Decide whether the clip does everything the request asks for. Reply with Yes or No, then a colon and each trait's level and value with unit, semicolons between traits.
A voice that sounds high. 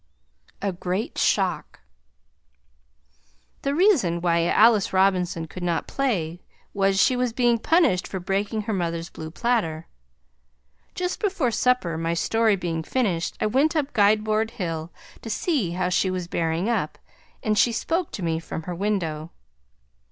Yes: high, 195 Hz